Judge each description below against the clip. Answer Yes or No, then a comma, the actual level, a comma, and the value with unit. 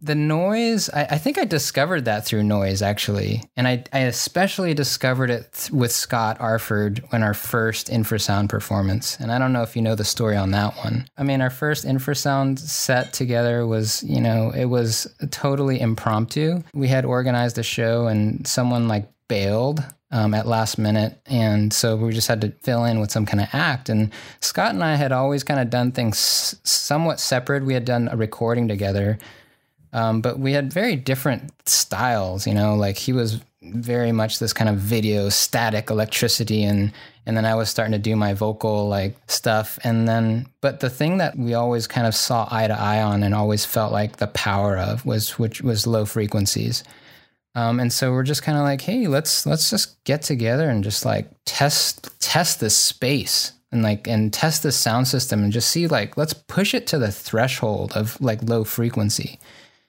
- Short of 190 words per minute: No, average, 200 wpm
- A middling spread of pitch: Yes, average, 3.7 semitones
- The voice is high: No, low, 115 Hz